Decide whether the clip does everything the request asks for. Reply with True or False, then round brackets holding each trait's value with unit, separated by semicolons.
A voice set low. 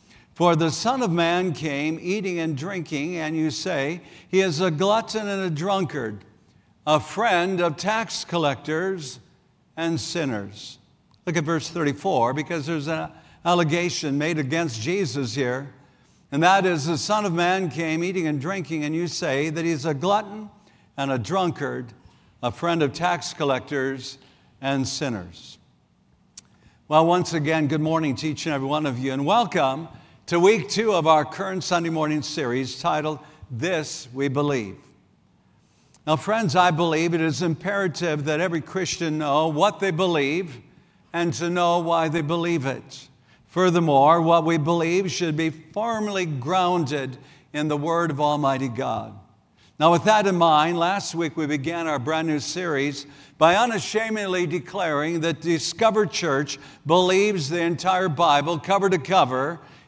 False (165 Hz)